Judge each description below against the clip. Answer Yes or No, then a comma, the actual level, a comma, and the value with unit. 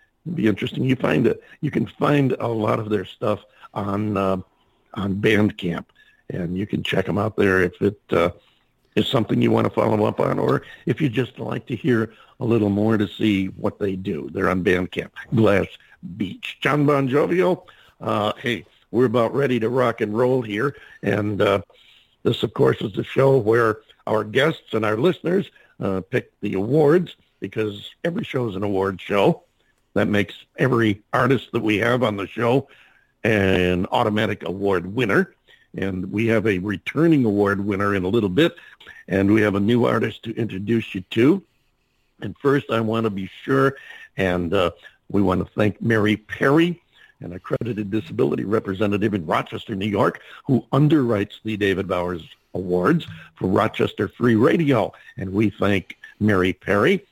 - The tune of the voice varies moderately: Yes, average, 4.3 semitones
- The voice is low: Yes, low, 110 Hz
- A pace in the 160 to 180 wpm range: Yes, average, 175 wpm